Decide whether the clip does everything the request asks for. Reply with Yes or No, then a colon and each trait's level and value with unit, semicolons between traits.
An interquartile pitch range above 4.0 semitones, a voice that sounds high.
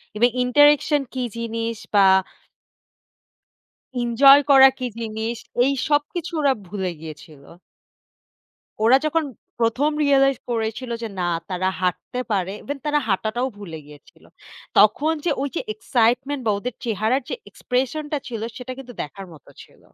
Yes: average, 4.5 semitones; high, 240 Hz